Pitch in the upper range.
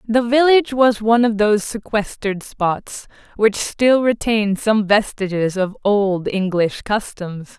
Yes: high, 215 Hz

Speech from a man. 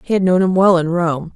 No: female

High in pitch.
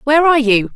Yes: very high, 275 Hz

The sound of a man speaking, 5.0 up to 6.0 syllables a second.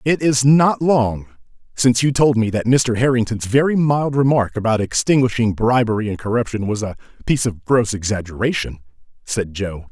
Yes: male; 5.2 syllables/s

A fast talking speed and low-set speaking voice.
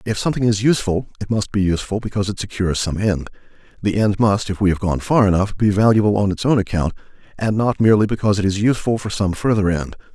Yes: fast, 230 wpm; low, 100 Hz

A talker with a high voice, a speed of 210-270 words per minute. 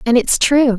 Yes: high, 245 Hz; fast, 230 wpm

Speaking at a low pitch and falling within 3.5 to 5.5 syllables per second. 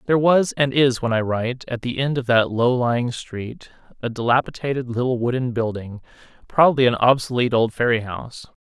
No: low, 125 Hz; 5.7 syllables/s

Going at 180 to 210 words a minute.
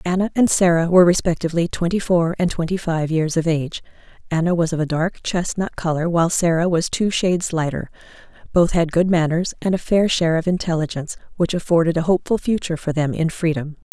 Yes: average, 195 wpm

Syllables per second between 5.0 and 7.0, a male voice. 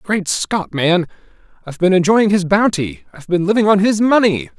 Yes: 5.2 syllables/s; male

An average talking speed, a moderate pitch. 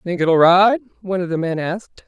No: fast, 230 wpm; medium, 180 Hz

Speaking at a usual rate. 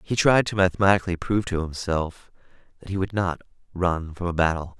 Yes: average, 190 wpm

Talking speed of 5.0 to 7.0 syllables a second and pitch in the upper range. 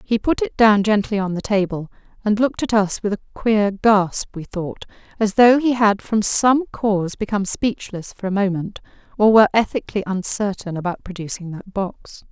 Yes: 5.1 syllables/s; high, 205 Hz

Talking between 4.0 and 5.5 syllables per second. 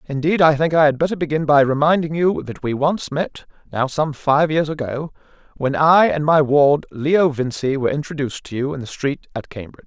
Yes: 5.4 syllables/s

